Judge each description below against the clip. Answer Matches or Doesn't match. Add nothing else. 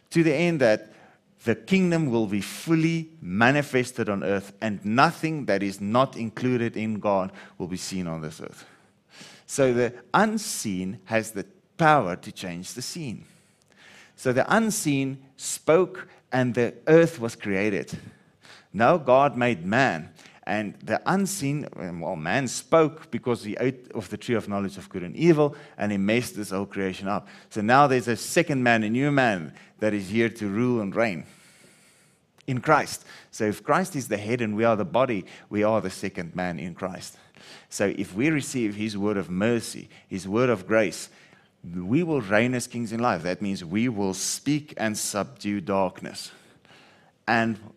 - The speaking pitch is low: Matches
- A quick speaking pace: Doesn't match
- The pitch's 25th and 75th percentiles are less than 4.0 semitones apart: Doesn't match